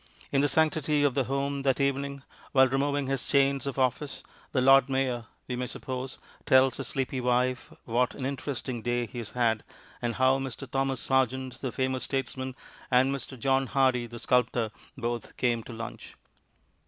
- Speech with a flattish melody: Yes, narrow, 1.6 semitones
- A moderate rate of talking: Yes, average, 175 wpm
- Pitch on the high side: No, low, 130 Hz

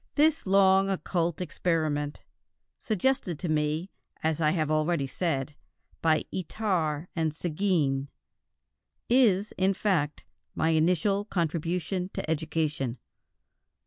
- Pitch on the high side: No, medium, 165 Hz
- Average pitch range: Yes, average, 3.7 semitones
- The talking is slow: Yes, slow, 105 wpm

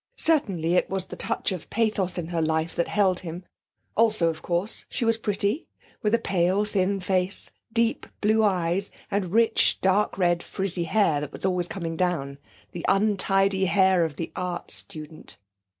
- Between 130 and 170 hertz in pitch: No, medium, 185 Hz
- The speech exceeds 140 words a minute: Yes, average, 170 wpm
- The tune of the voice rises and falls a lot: No, average, 3.1 semitones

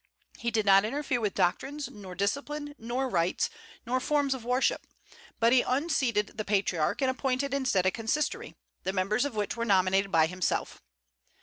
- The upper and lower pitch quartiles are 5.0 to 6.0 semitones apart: Yes, wide, 5.4 semitones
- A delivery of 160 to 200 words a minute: Yes, average, 170 wpm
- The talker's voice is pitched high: Yes, high, 230 Hz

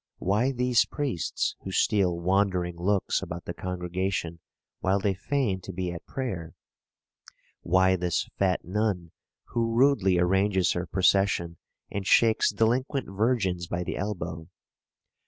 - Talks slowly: Yes, slow, 130 wpm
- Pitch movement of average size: Yes, average, 3.2 semitones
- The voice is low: Yes, very low, 95 Hz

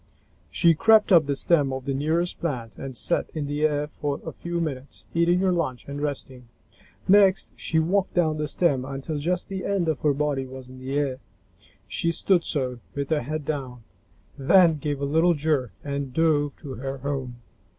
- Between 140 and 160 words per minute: No, average, 190 wpm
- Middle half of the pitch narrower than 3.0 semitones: No, average, 3.7 semitones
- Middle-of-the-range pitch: Yes, medium, 145 Hz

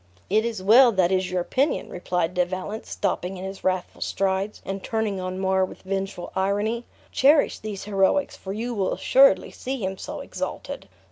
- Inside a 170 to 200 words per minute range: Yes, average, 180 wpm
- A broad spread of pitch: No, average, 2.8 semitones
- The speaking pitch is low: No, high, 195 Hz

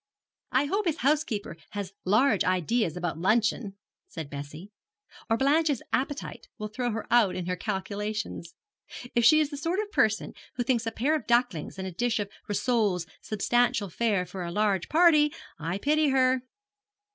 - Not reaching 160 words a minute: No, average, 170 wpm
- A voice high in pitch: Yes, high, 220 Hz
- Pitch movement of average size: No, wide, 5.8 semitones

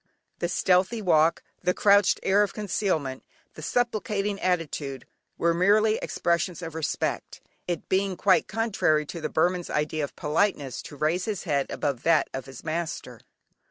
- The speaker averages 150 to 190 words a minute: Yes, average, 155 wpm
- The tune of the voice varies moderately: Yes, average, 4.5 semitones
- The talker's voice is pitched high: No, medium, 175 Hz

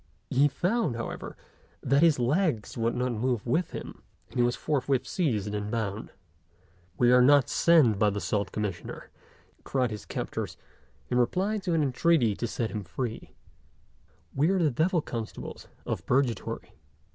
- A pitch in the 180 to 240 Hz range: No, low, 125 Hz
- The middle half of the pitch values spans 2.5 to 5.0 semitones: No, wide, 5.5 semitones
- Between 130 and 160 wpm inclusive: Yes, average, 155 wpm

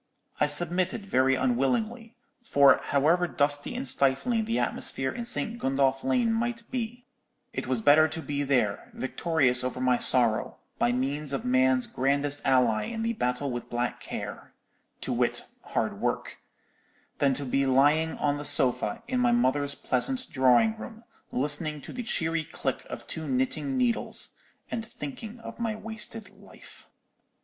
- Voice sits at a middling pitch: Yes, medium, 145 Hz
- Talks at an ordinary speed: Yes, average, 150 wpm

